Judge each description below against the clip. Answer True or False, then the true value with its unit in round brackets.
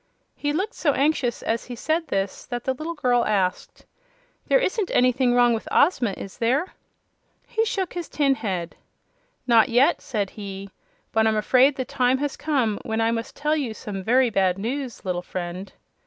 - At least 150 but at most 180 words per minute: True (160 wpm)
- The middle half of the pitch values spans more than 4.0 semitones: True (4.7 semitones)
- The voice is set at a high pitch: True (245 Hz)